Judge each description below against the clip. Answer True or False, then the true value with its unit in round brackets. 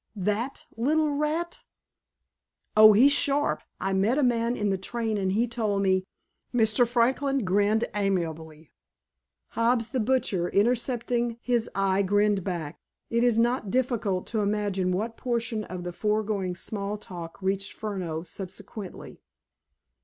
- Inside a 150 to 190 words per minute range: False (135 wpm)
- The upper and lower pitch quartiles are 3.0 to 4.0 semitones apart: True (3.7 semitones)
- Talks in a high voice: True (215 Hz)